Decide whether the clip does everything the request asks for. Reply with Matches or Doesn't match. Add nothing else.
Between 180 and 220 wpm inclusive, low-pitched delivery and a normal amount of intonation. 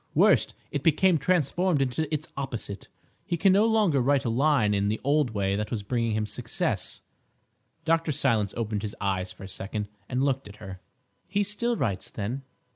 Doesn't match